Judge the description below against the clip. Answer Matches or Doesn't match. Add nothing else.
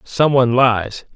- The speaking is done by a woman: Doesn't match